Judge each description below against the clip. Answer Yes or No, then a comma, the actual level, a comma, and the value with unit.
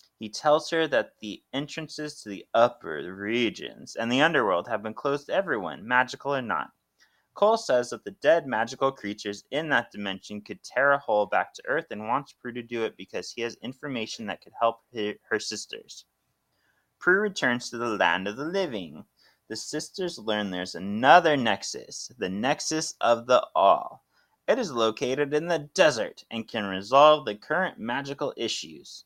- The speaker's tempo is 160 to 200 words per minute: Yes, average, 175 wpm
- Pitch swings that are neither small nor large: No, wide, 5.8 semitones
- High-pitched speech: No, low, 120 Hz